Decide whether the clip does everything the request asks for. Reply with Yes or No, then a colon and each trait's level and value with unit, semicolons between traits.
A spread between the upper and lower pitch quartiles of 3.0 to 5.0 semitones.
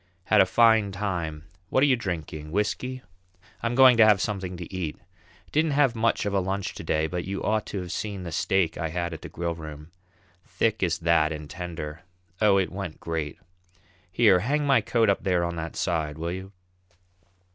Yes: average, 4.4 semitones